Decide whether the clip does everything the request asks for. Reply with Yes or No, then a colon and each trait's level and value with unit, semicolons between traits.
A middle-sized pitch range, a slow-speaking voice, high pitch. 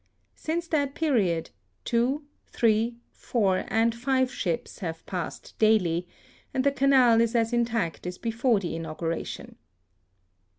No: wide, 6.1 semitones; slow, 125 wpm; high, 230 Hz